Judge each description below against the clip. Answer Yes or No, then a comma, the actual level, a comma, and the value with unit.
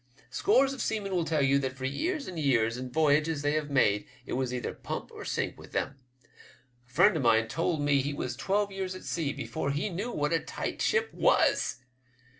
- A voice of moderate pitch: Yes, medium, 150 Hz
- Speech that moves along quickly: Yes, fast, 215 wpm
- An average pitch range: No, wide, 6.0 semitones